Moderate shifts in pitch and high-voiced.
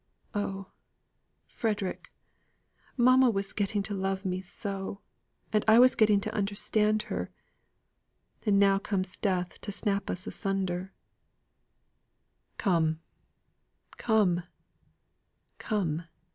No: narrow, 1.9 semitones; high, 200 Hz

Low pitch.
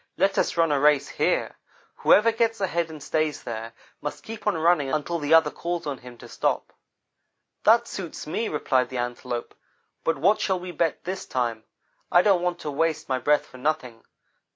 No: medium, 155 Hz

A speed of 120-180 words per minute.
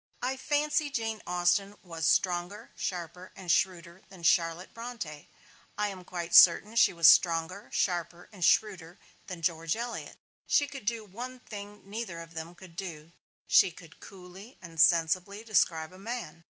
Yes: average, 155 wpm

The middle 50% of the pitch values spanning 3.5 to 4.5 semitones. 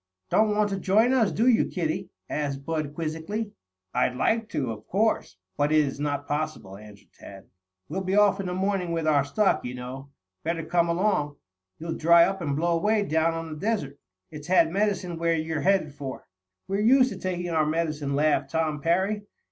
No: average, 4.9 semitones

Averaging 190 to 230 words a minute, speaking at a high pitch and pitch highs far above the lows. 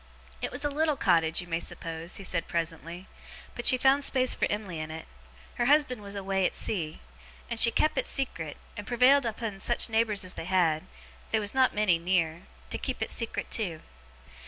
Yes: average, 200 wpm; high, 200 Hz; wide, 6.2 semitones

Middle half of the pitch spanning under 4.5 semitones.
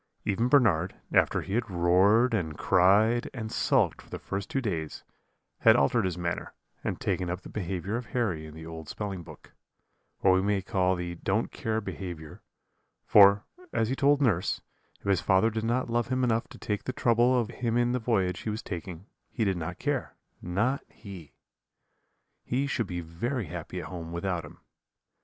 No: average, 4.8 semitones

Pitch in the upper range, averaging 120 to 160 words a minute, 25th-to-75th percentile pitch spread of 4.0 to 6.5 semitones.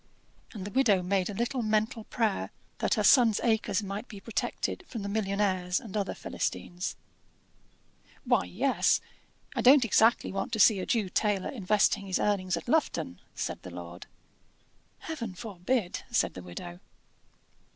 No: high, 205 Hz; average, 150 wpm; average, 3.6 semitones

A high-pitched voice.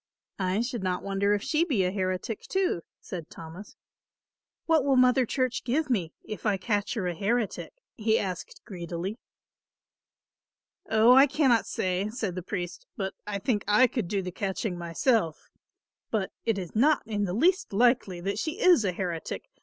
Yes: high, 205 Hz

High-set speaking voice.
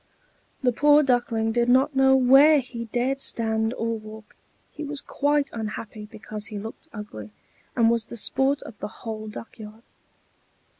Yes: high, 230 Hz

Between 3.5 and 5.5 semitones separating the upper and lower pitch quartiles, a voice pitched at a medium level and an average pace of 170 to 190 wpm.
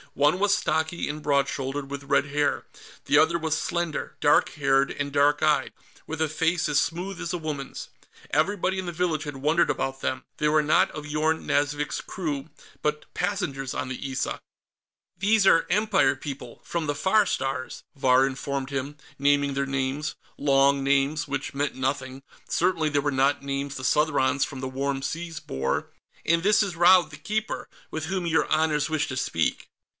No: average, 2.8 semitones; medium, 145 Hz; average, 180 wpm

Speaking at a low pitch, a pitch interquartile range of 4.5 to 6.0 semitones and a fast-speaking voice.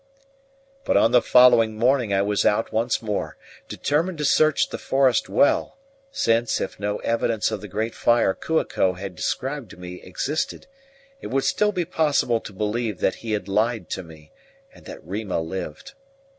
No: low, 115 Hz; average, 4.9 semitones; average, 175 wpm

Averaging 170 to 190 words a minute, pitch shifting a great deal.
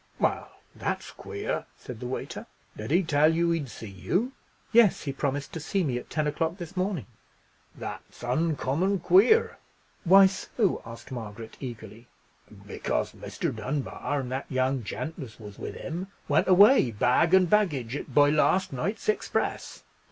No: average, 155 wpm; wide, 6.8 semitones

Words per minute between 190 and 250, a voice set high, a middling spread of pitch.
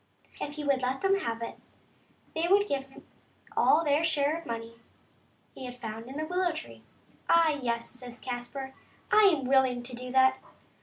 Yes: fast, 205 wpm; very high, 265 Hz; average, 4.3 semitones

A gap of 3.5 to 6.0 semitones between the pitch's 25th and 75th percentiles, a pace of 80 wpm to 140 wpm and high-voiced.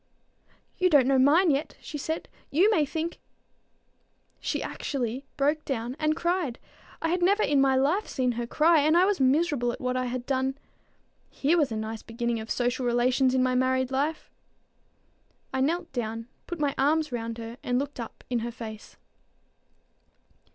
No: average, 4.2 semitones; average, 175 wpm; very high, 265 Hz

